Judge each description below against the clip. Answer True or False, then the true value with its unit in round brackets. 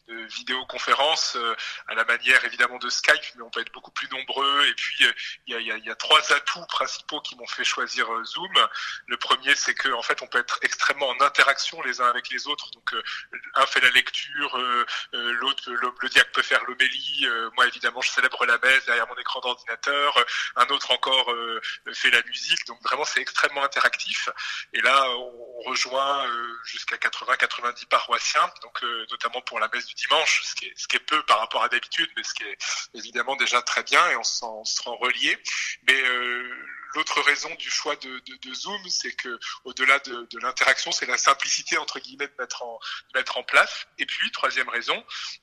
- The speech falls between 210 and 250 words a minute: True (215 wpm)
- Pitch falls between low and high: False (130 Hz)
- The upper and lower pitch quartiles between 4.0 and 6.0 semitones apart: False (2.8 semitones)